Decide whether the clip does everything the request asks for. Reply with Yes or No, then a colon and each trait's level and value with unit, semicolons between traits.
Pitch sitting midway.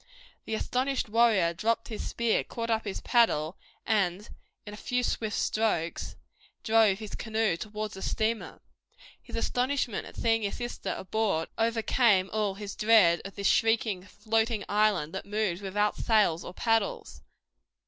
No: high, 215 Hz